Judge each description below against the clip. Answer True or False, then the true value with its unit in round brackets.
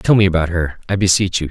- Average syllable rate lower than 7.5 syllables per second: True (6.5 syllables/s)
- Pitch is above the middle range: False (90 Hz)